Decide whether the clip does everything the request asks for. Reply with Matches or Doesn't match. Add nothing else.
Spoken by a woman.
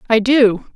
Matches